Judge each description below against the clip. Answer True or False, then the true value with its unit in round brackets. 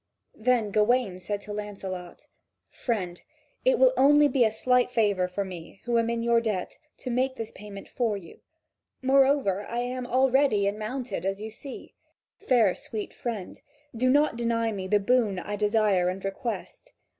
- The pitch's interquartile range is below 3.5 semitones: False (4.0 semitones)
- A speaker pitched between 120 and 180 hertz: False (225 Hz)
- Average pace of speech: True (170 wpm)